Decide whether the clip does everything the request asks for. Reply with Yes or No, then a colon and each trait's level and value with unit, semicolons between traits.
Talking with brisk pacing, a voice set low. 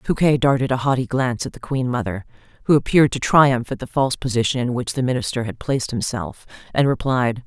Yes: fast, 210 wpm; low, 125 Hz